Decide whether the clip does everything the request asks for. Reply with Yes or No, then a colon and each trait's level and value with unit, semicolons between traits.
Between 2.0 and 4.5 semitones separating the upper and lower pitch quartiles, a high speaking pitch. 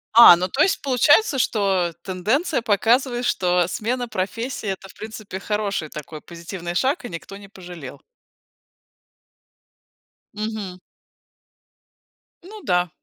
No: average, 5.2 semitones; high, 205 Hz